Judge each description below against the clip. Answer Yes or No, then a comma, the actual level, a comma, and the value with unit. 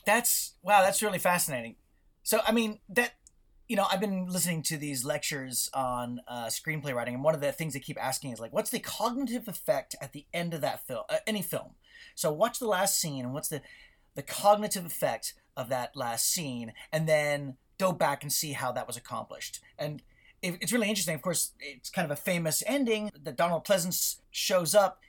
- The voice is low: No, medium, 170 Hz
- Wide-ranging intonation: Yes, wide, 6.2 semitones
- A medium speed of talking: No, fast, 210 wpm